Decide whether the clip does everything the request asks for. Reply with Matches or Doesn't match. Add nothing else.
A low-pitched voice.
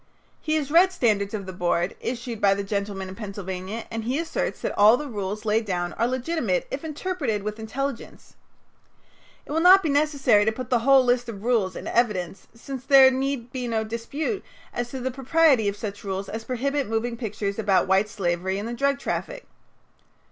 Doesn't match